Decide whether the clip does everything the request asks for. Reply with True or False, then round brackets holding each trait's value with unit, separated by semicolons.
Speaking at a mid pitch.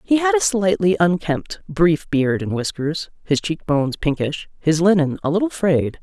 True (170 Hz)